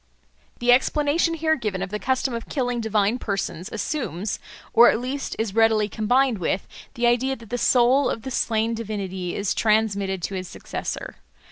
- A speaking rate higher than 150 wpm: Yes, average, 170 wpm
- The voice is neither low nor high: No, high, 225 Hz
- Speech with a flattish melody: No, average, 3.8 semitones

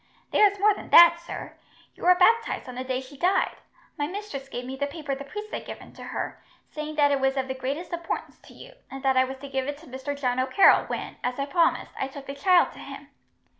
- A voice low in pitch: No, very high, 280 Hz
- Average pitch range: Yes, average, 4.5 semitones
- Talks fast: Yes, fast, 250 wpm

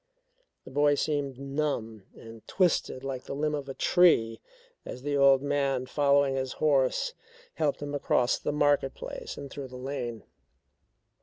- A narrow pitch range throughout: Yes, narrow, 2.0 semitones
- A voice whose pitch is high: No, medium, 140 Hz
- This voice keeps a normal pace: Yes, average, 155 wpm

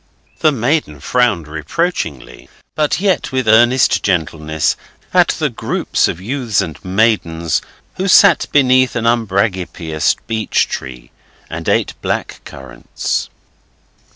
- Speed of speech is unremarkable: No, slow, 115 wpm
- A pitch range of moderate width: No, wide, 8.1 semitones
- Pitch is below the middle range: Yes, low, 110 Hz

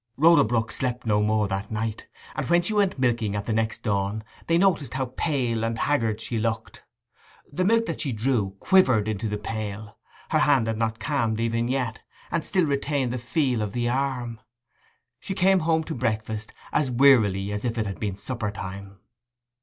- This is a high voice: No, low, 115 Hz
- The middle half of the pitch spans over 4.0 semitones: Yes, average, 4.4 semitones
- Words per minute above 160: Yes, average, 185 wpm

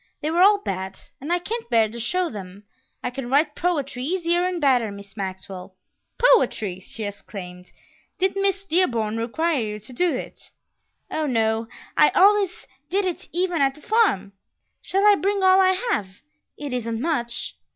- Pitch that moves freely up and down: Yes, wide, 8.9 semitones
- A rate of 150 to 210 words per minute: Yes, average, 170 wpm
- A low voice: No, very high, 280 Hz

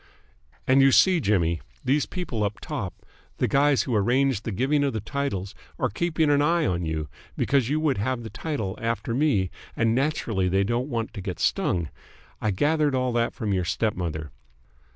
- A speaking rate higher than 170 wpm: Yes, average, 180 wpm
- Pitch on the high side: No, low, 120 Hz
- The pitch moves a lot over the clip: Yes, wide, 6.3 semitones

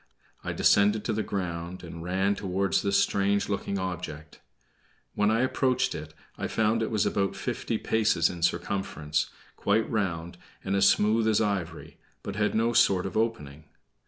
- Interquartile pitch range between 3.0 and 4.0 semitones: Yes, average, 3.6 semitones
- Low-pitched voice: Yes, low, 100 Hz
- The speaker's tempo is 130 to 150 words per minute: No, average, 160 wpm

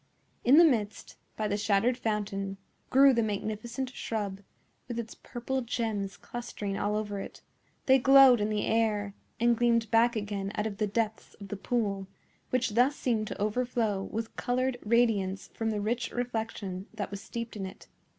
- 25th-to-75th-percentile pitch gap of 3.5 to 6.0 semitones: No, average, 2.9 semitones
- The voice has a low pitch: No, high, 220 Hz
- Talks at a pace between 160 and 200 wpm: Yes, average, 170 wpm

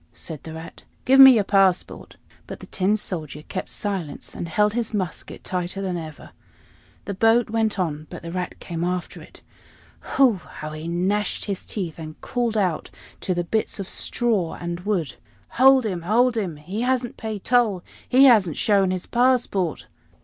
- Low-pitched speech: No, high, 195 Hz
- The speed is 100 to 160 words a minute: No, average, 175 wpm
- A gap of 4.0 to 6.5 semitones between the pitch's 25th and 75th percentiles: Yes, average, 4.5 semitones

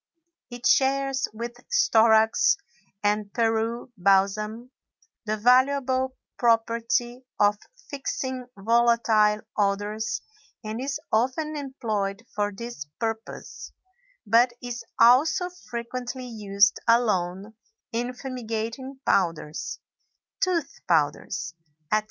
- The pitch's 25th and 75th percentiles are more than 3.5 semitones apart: No, average, 3.2 semitones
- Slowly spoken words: Yes, slow, 90 wpm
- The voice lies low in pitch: No, high, 230 Hz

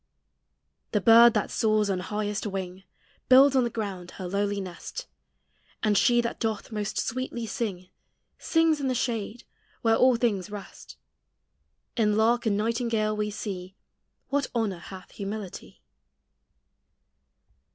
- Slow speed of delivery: Yes, slow, 130 wpm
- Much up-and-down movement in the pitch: No, average, 2.9 semitones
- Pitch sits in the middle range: No, high, 215 Hz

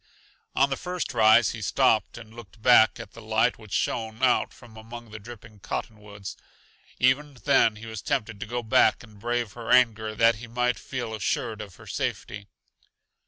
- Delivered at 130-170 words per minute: No, average, 180 wpm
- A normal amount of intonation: No, narrow, 2.0 semitones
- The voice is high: No, low, 115 Hz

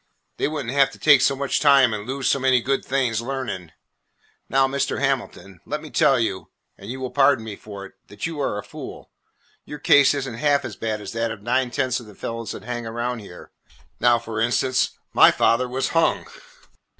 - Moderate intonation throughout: Yes, average, 3.3 semitones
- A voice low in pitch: Yes, low, 125 Hz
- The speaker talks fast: Yes, fast, 215 wpm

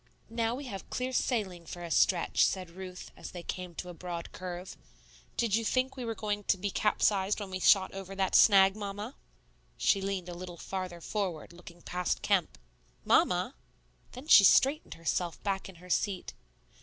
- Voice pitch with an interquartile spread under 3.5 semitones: Yes, average, 2.8 semitones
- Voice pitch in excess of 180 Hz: Yes, high, 190 Hz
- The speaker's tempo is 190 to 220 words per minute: No, average, 180 wpm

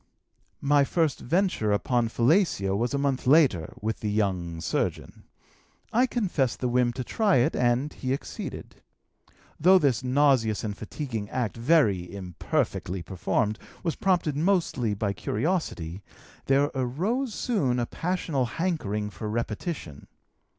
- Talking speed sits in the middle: No, slow, 130 wpm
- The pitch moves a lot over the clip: Yes, wide, 7.0 semitones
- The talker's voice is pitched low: Yes, low, 125 Hz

